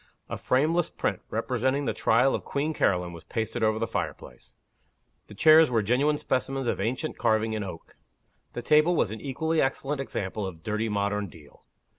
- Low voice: Yes, low, 115 Hz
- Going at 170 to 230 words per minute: Yes, average, 175 wpm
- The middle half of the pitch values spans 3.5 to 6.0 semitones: Yes, average, 5.2 semitones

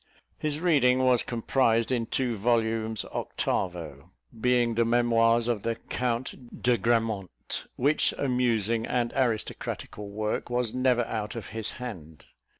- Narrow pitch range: Yes, narrow, 2.0 semitones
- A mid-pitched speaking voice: No, low, 115 Hz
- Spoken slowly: Yes, slow, 130 wpm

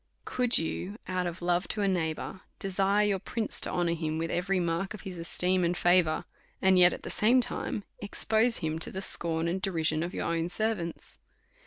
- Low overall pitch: No, medium, 180 Hz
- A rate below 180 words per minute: No, average, 195 wpm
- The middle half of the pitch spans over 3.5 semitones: No, average, 2.8 semitones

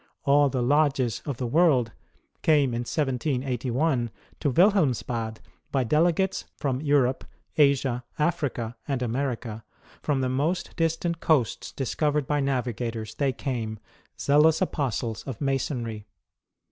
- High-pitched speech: No, low, 135 Hz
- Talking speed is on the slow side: Yes, slow, 120 wpm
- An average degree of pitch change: Yes, average, 3.6 semitones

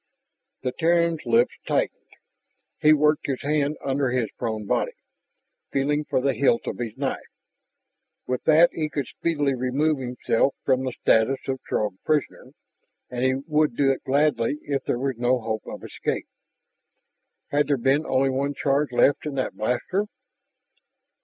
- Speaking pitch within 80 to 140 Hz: Yes, low, 135 Hz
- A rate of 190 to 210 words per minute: No, average, 155 wpm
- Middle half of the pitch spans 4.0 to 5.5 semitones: No, average, 3.0 semitones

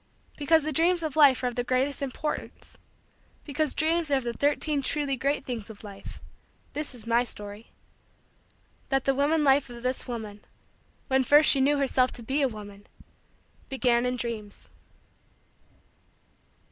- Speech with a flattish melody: No, average, 3.5 semitones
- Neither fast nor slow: Yes, average, 160 wpm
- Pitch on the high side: Yes, very high, 265 Hz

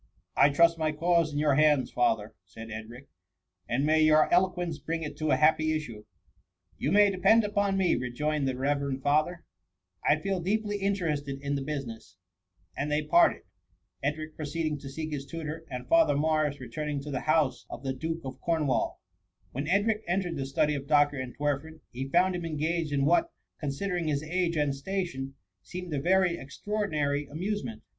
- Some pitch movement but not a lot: Yes, average, 3.6 semitones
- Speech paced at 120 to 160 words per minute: No, average, 190 wpm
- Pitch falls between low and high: Yes, medium, 150 Hz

